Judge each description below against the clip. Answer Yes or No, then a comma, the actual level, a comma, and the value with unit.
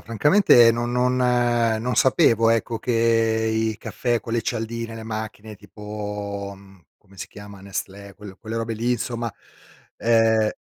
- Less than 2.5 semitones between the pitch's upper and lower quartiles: Yes, narrow, 2.0 semitones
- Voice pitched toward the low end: Yes, low, 115 Hz